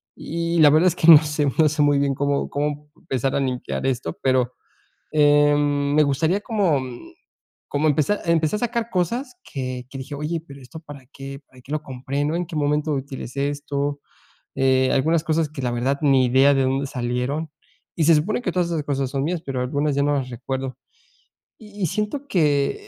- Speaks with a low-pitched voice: No, medium, 145 Hz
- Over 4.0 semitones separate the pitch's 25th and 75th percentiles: No, average, 3.0 semitones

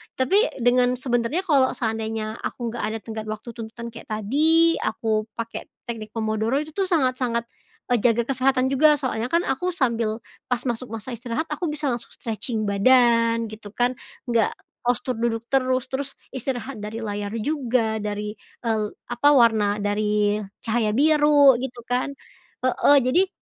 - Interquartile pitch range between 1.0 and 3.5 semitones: Yes, average, 3.1 semitones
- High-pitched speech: Yes, high, 235 Hz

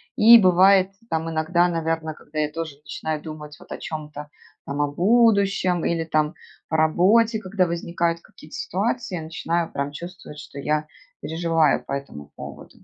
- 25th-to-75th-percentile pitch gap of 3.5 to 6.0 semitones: No, average, 3.1 semitones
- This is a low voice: No, medium, 165 Hz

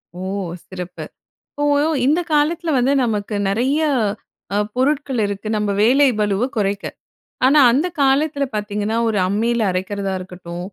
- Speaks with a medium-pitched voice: No, high, 220 Hz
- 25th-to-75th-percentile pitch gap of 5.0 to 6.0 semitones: Yes, wide, 5.6 semitones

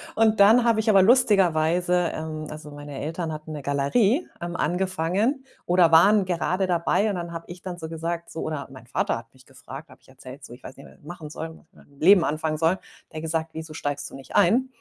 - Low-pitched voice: No, medium, 165 Hz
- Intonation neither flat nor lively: Yes, average, 3.7 semitones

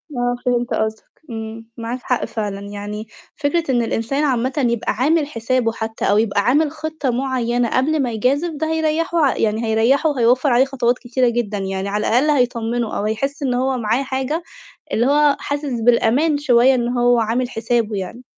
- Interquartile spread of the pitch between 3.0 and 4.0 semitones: Yes, average, 3.5 semitones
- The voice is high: Yes, high, 245 Hz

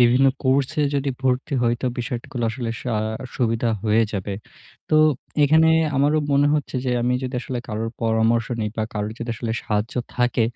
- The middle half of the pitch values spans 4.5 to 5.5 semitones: No, average, 3.1 semitones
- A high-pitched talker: No, low, 120 Hz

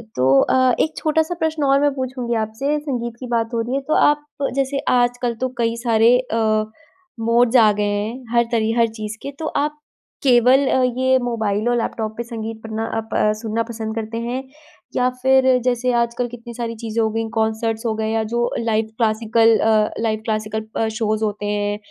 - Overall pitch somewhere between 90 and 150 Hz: No, high, 230 Hz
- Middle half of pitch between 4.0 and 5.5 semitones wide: No, narrow, 2.4 semitones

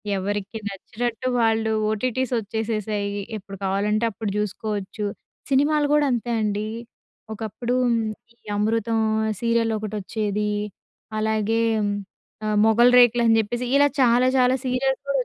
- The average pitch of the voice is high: Yes, high, 220 Hz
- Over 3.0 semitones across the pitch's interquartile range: No, narrow, 2.5 semitones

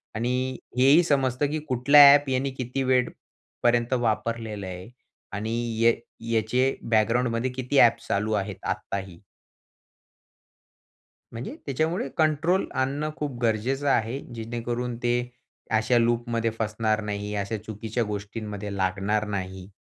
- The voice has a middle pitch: No, low, 115 Hz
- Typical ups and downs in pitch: Yes, average, 3.3 semitones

